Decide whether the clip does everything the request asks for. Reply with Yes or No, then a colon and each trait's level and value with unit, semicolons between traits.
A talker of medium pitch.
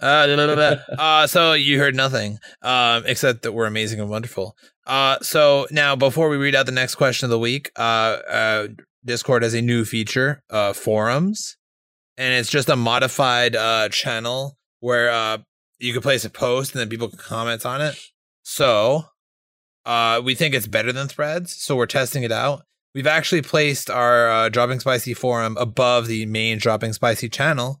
No: low, 125 Hz